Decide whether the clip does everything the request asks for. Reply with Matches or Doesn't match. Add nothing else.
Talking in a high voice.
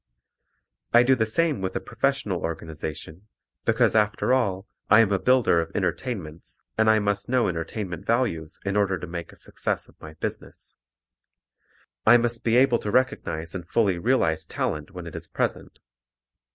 Doesn't match